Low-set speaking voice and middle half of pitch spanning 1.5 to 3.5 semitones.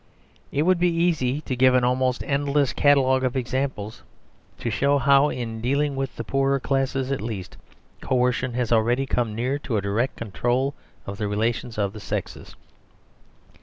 Yes: low, 130 Hz; average, 2.9 semitones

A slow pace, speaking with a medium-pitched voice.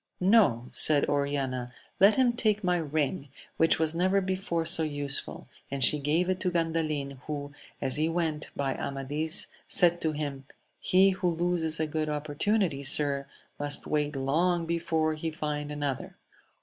No: average, 155 wpm; medium, 155 Hz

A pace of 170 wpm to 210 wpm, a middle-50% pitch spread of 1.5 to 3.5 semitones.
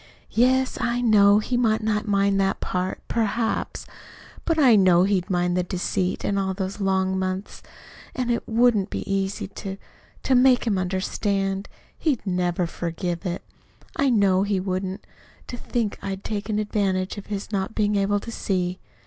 No: average, 160 wpm; average, 2.7 semitones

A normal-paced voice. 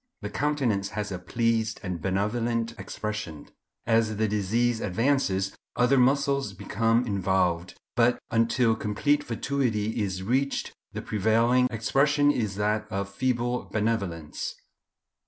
No: slow, 120 wpm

